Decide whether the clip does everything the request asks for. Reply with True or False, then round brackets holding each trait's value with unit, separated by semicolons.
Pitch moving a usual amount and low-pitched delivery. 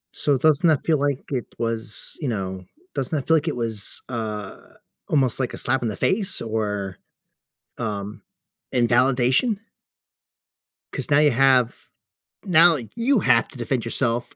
True (4.5 semitones; 125 Hz)